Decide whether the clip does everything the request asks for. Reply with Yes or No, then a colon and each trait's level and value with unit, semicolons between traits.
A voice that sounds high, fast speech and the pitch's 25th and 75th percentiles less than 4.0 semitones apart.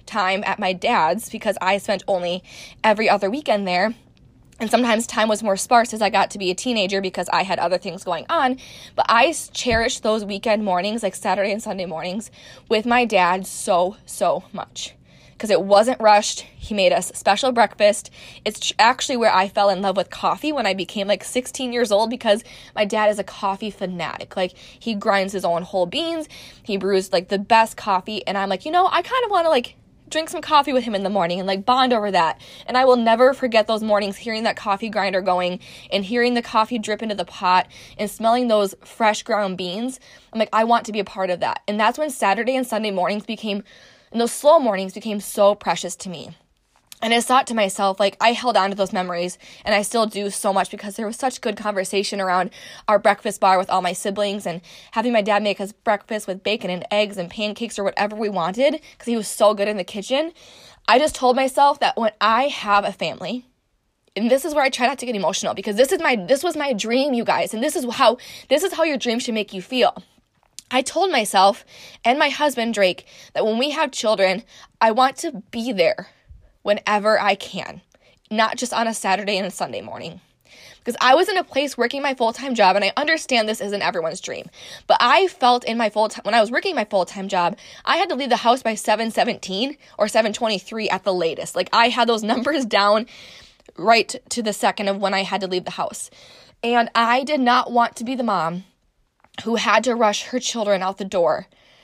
Yes: high, 215 Hz; fast, 225 wpm; average, 3.6 semitones